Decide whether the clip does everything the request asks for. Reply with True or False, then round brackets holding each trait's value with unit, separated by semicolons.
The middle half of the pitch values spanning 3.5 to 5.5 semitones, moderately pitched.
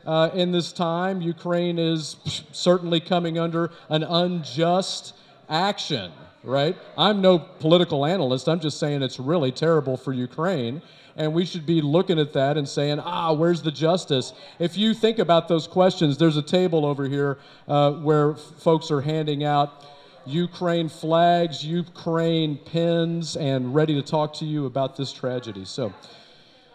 False (2.9 semitones; 160 Hz)